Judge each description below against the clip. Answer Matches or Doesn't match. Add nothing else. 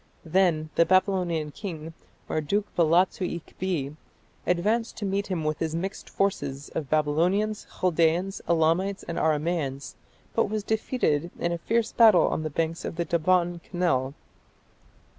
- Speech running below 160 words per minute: Matches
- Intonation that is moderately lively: Matches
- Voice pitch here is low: Doesn't match